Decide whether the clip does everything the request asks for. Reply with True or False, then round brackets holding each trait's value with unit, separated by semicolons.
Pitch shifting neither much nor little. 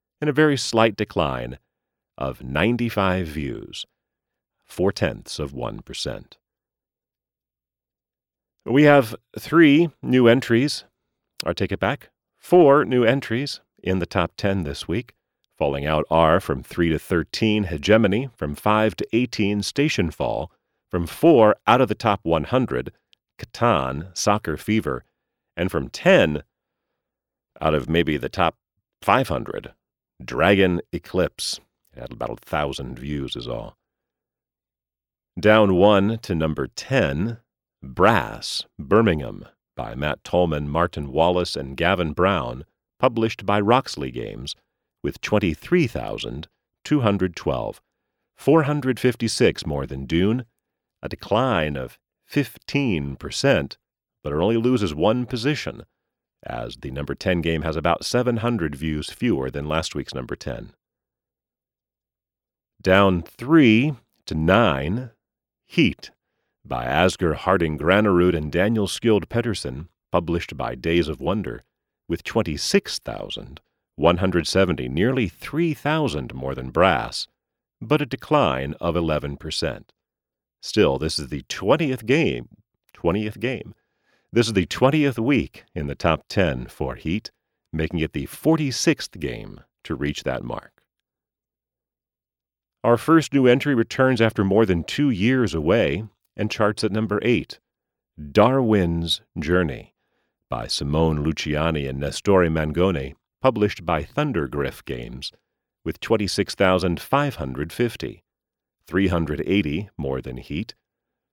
False (7.3 semitones)